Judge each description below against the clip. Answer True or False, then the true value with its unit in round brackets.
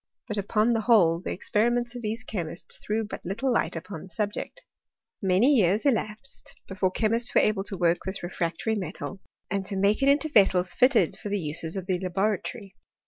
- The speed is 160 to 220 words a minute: True (190 wpm)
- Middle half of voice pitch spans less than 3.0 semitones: False (3.6 semitones)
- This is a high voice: True (205 Hz)